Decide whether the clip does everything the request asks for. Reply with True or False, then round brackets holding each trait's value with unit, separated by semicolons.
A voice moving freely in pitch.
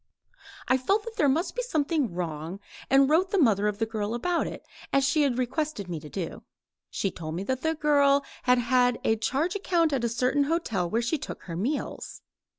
True (6.4 semitones)